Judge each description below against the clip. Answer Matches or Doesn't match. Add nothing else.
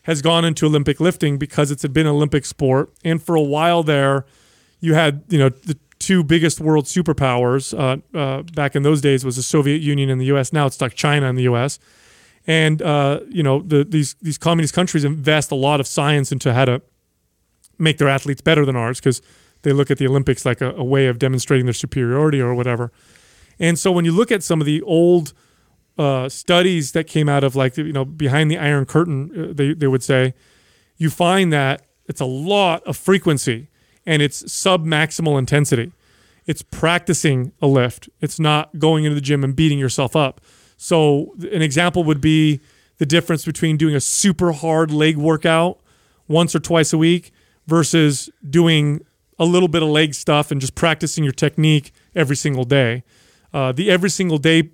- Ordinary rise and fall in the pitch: Matches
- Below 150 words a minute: Doesn't match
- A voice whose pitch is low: Doesn't match